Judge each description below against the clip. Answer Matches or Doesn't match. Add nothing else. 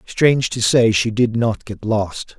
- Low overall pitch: Matches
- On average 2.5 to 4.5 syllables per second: Matches